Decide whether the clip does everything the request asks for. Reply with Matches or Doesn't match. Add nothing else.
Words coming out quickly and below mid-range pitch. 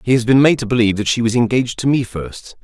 Matches